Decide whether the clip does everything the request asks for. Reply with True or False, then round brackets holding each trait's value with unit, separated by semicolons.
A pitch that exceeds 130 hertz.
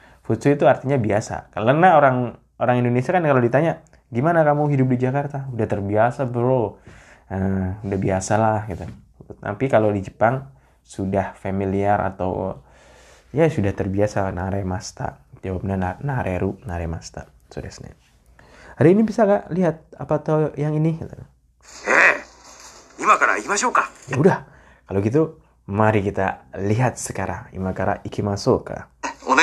False (110 Hz)